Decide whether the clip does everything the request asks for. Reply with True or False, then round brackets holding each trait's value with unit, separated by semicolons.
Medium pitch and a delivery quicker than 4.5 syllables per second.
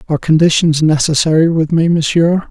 True (160 Hz; 5.6 syllables/s)